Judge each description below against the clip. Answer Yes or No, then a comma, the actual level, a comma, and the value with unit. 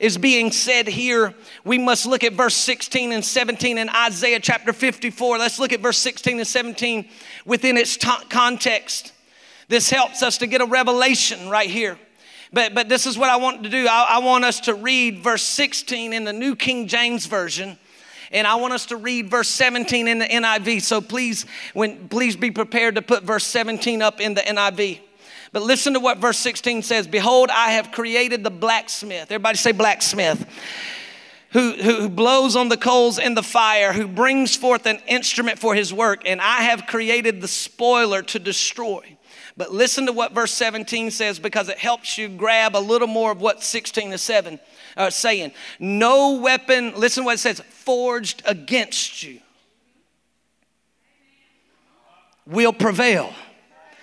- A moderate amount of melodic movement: No, narrow, 2.2 semitones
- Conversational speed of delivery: Yes, average, 180 wpm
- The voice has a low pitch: No, high, 235 Hz